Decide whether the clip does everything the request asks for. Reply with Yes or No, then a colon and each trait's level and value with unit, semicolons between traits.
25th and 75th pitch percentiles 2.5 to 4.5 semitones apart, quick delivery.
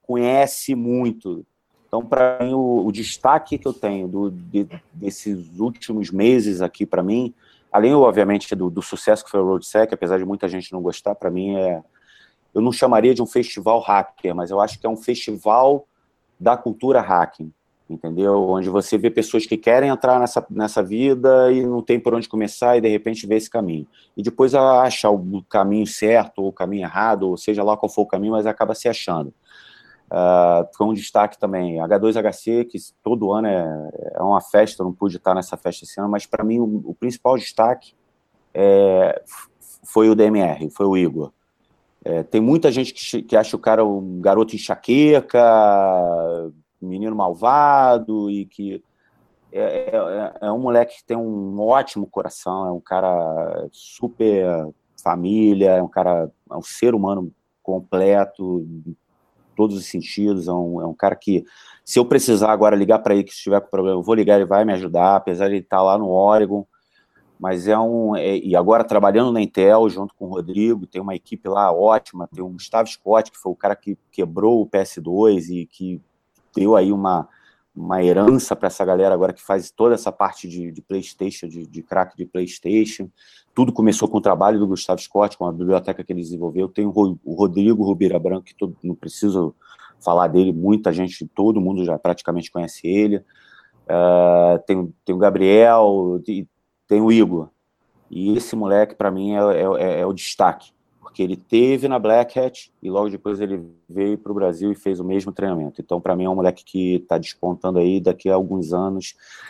Yes: average, 3.1 semitones; fast, 190 wpm